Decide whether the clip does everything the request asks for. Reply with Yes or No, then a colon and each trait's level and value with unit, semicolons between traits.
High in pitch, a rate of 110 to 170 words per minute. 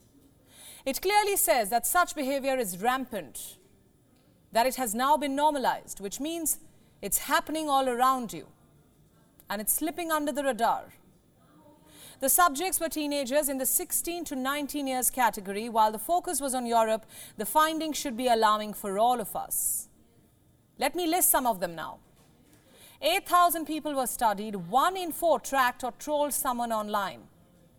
Yes: very high, 265 Hz; average, 155 wpm